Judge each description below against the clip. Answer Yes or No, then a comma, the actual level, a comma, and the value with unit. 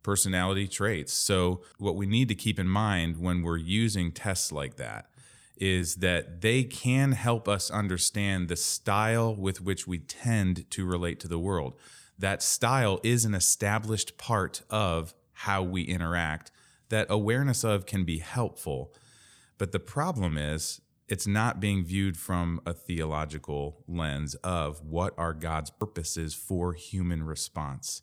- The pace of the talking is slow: No, average, 150 wpm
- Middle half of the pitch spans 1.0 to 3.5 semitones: No, average, 4.0 semitones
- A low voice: Yes, very low, 95 Hz